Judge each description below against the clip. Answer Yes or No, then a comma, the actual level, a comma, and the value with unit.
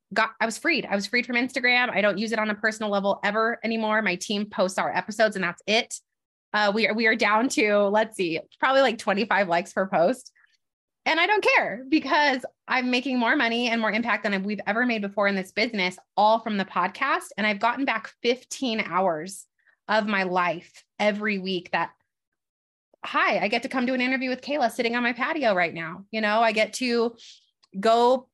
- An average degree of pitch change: Yes, average, 3.6 semitones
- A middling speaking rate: No, fast, 215 wpm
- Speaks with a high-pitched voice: Yes, high, 220 Hz